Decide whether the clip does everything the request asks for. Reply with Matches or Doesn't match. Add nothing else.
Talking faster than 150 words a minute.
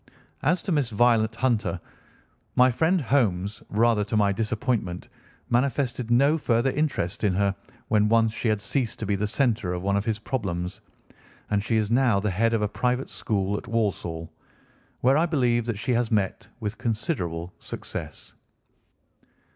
Matches